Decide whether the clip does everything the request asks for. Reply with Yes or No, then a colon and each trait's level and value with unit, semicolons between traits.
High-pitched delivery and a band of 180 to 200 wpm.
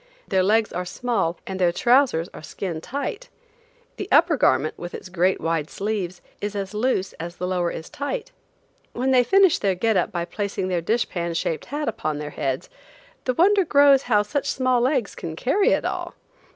Yes: high, 205 Hz; average, 190 wpm